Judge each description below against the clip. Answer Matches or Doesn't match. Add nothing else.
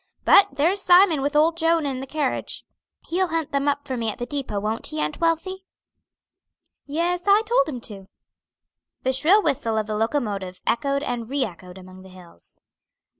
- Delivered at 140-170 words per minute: Doesn't match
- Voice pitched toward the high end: Matches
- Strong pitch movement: Matches